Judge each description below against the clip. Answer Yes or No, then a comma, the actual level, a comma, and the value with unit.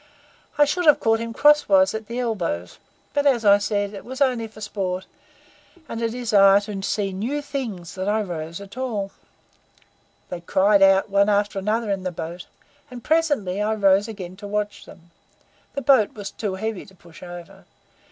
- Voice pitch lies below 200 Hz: No, high, 205 Hz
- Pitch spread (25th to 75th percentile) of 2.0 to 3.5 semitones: Yes, average, 3.2 semitones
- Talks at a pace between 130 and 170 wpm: No, average, 180 wpm